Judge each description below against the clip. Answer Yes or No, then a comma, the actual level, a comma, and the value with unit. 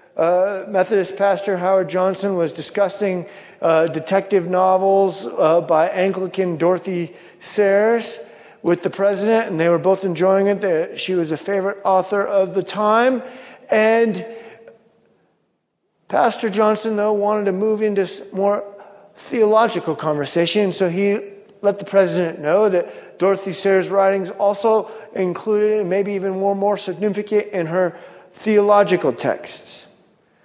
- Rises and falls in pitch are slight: Yes, narrow, 2.1 semitones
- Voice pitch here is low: No, high, 195 Hz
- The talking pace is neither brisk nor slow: No, slow, 130 wpm